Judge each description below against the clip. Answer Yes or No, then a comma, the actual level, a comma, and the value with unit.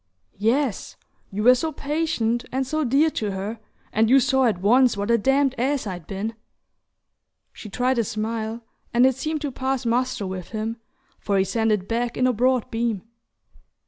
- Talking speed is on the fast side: No, average, 180 wpm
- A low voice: No, high, 235 Hz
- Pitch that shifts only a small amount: No, average, 3.5 semitones